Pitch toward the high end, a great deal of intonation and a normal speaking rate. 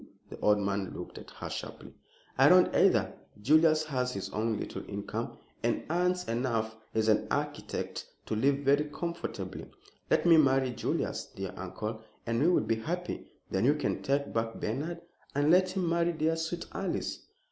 No: medium, 140 Hz; wide, 6.8 semitones; average, 170 wpm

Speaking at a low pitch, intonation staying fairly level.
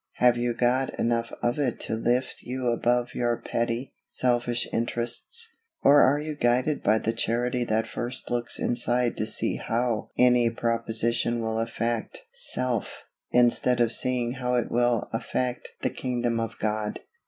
Yes: low, 120 Hz; narrow, 1.2 semitones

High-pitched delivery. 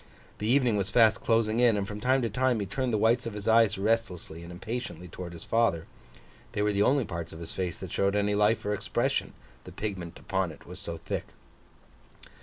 No: low, 105 Hz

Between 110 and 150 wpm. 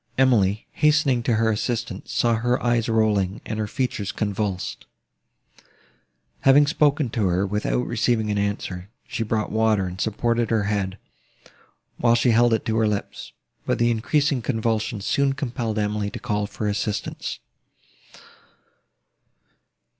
Yes: average, 140 wpm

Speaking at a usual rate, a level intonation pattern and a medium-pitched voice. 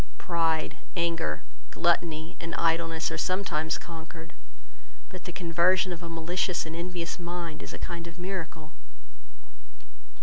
No: slow, 130 wpm; narrow, 1.3 semitones; medium, 170 Hz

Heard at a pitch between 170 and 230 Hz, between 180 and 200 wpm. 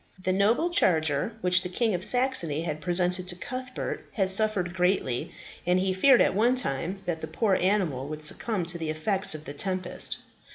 Yes: medium, 185 Hz; average, 190 wpm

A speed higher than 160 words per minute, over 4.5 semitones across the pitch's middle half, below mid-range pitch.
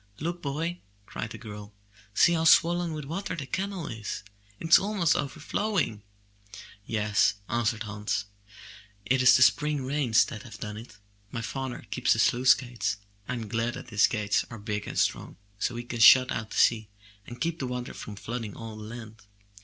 Yes: average, 180 wpm; wide, 5.4 semitones; low, 120 Hz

